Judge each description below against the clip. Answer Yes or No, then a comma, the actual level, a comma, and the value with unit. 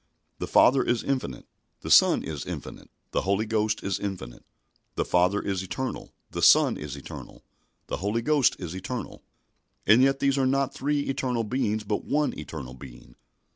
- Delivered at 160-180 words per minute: Yes, average, 170 wpm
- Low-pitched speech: Yes, low, 110 Hz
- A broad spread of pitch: Yes, wide, 6.2 semitones